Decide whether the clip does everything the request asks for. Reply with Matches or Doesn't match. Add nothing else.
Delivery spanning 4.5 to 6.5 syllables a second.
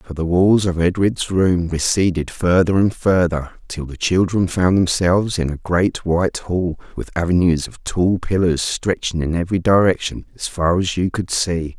Matches